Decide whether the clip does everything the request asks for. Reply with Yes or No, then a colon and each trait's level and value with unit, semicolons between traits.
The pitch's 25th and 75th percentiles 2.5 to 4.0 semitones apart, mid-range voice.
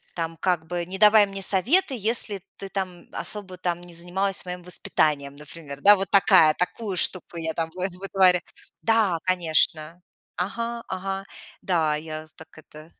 Yes: average, 3.2 semitones; medium, 180 Hz